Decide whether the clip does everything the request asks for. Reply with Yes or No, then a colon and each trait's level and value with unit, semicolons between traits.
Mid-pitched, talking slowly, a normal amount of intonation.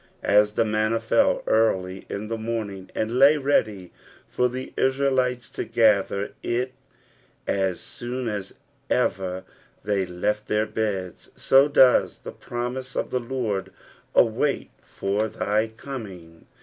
No: low, 110 Hz; slow, 130 wpm; average, 3.9 semitones